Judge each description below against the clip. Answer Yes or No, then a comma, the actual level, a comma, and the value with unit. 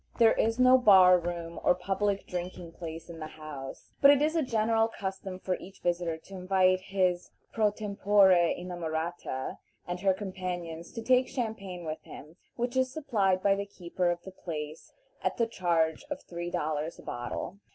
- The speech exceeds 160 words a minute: Yes, average, 175 wpm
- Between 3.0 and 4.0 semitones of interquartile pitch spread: Yes, average, 3.4 semitones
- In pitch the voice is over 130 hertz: Yes, medium, 185 Hz